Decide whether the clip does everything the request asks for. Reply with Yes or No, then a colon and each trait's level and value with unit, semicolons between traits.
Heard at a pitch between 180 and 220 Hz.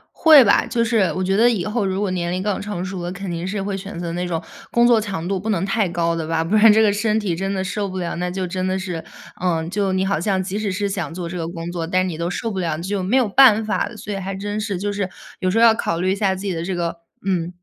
Yes: high, 190 Hz